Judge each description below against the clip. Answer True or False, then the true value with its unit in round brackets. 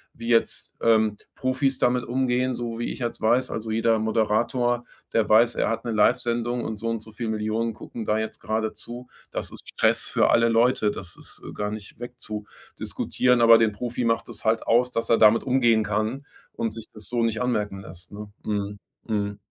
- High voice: False (115 Hz)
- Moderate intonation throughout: False (2.0 semitones)